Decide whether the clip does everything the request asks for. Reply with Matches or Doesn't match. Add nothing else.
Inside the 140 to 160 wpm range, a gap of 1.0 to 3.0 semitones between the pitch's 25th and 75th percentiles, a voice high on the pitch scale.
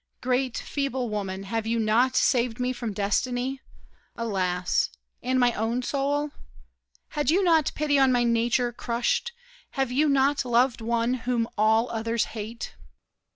Matches